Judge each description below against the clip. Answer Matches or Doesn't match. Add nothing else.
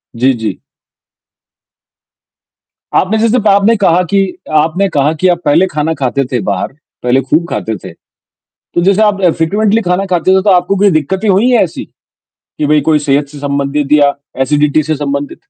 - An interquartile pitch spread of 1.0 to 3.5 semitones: Doesn't match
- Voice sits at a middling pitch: Matches